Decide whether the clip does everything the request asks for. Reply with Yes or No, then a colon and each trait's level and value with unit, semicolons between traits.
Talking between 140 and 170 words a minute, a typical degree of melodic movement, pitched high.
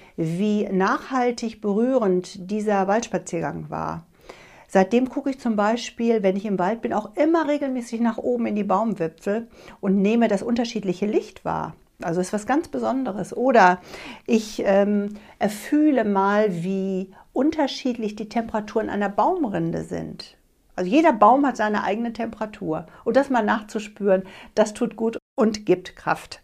Yes: average, 145 wpm; average, 3.7 semitones; high, 215 Hz